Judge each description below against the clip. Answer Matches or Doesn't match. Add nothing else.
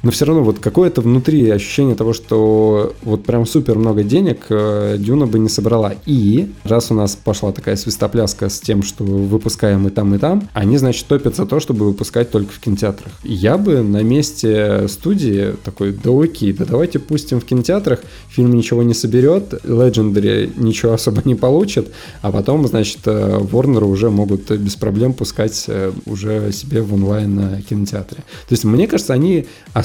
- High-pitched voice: Doesn't match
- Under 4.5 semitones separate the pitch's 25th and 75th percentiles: Matches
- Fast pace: Matches